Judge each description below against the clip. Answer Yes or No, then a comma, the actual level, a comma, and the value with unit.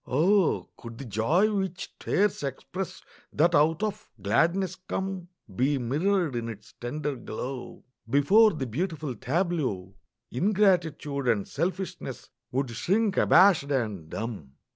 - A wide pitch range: Yes, wide, 7.4 semitones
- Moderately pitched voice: Yes, medium, 150 Hz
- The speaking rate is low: Yes, slow, 120 wpm